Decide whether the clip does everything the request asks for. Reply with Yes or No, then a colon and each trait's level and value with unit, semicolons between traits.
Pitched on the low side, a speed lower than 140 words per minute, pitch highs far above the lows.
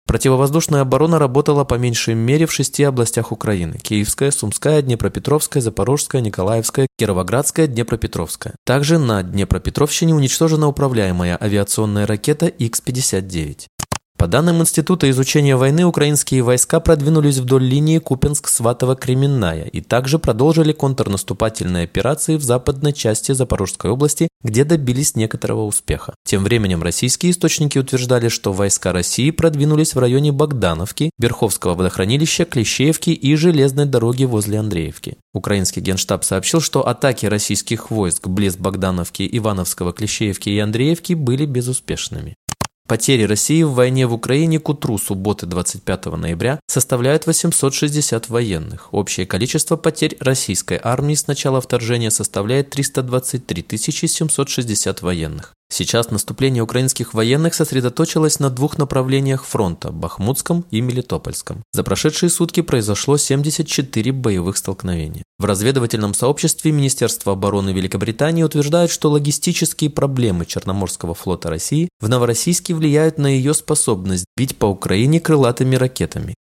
Yes: low, 125 Hz; average, 120 wpm; wide, 6.0 semitones